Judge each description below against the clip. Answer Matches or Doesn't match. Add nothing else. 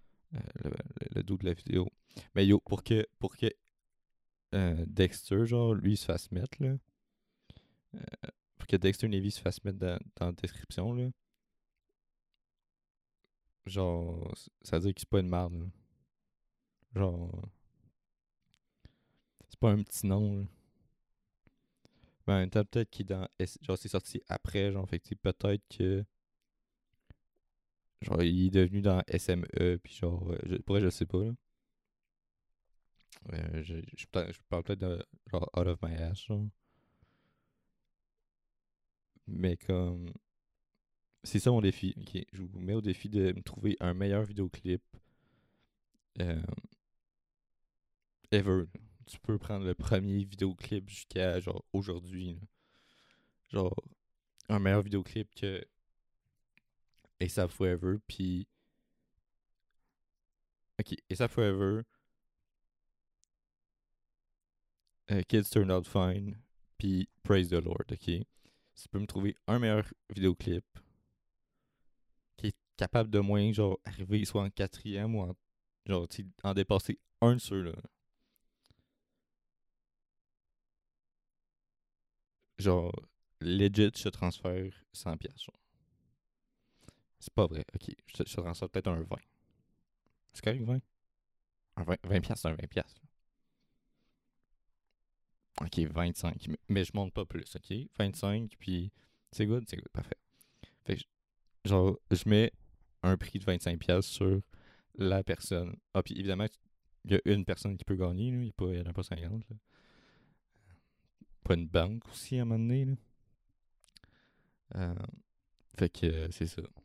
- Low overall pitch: Matches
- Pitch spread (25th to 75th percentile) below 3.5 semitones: Matches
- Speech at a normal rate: Doesn't match